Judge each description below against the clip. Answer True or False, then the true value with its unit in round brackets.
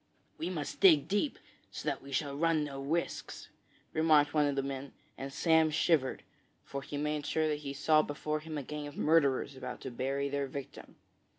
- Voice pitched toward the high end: False (145 Hz)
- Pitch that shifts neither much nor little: False (2.2 semitones)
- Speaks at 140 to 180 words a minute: False (195 wpm)